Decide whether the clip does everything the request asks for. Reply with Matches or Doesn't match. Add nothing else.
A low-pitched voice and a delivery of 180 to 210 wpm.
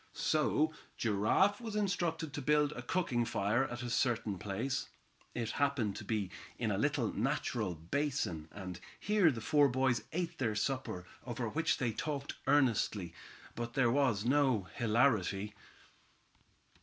Doesn't match